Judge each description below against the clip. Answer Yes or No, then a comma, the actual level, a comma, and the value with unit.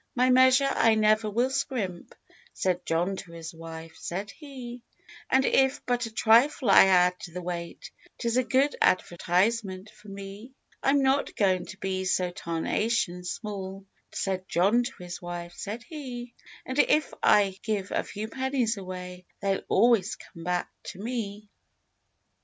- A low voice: No, high, 205 Hz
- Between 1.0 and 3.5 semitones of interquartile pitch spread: No, average, 5.1 semitones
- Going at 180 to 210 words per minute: No, average, 155 wpm